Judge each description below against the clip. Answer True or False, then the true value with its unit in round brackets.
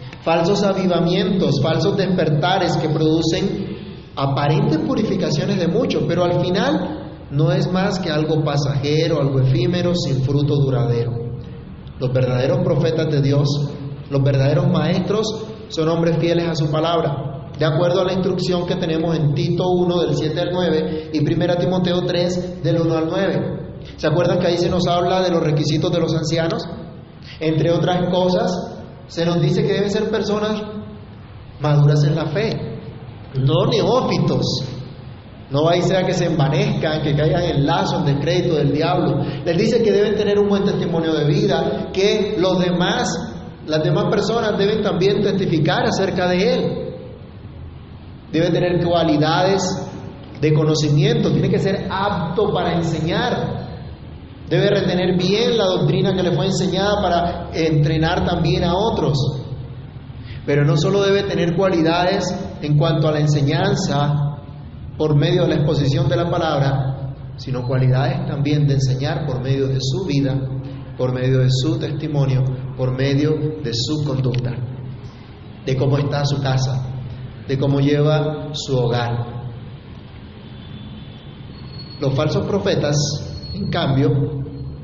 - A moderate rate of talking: True (145 wpm)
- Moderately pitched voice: True (160 Hz)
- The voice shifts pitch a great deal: False (4.2 semitones)